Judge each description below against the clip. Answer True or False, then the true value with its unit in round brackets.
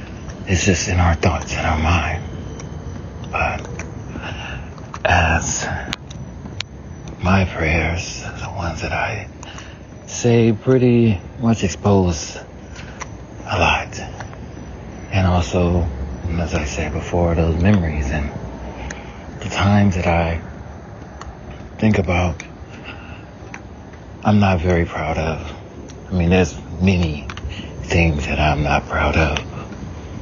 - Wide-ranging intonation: False (3.7 semitones)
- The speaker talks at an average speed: False (105 wpm)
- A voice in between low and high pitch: False (90 Hz)